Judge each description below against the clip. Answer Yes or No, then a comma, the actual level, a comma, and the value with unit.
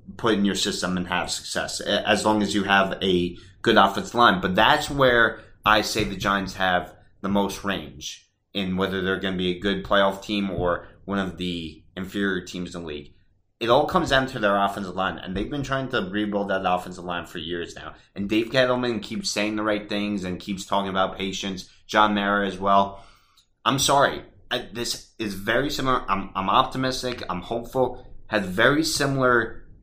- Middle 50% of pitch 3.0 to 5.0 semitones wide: No, narrow, 2.4 semitones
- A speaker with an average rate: Yes, average, 195 wpm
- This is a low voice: Yes, low, 100 Hz